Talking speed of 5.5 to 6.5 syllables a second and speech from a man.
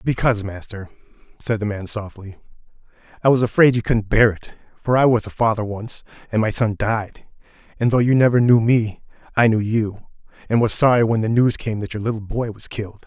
Yes: 5.6 syllables/s; male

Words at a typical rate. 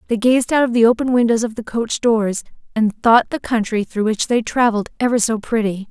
No: fast, 225 wpm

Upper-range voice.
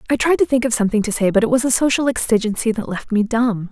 Yes: high, 230 Hz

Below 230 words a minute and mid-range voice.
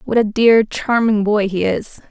No: average, 200 wpm; high, 215 Hz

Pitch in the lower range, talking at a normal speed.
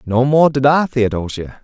Yes: low, 130 Hz; average, 185 wpm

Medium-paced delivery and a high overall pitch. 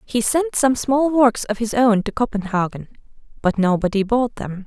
Yes: average, 180 wpm; high, 225 Hz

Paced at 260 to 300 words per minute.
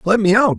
No: fast, 310 wpm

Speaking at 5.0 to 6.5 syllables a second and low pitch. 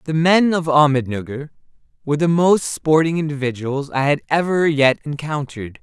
No: 5.2 syllables/s; medium, 150 Hz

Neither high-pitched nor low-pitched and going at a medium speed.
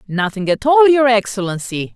No: high, 225 Hz; average, 155 wpm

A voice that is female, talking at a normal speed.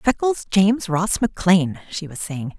Yes: female; average, 160 wpm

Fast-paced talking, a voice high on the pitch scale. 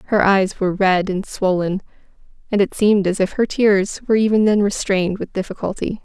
No: average, 190 wpm; high, 195 Hz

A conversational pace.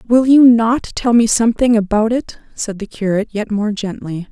Yes: average, 195 wpm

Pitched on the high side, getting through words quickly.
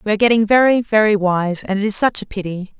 Yes: high, 210 Hz; fast, 260 wpm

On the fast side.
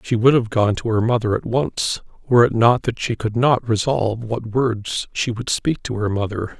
Yes: fast, 225 wpm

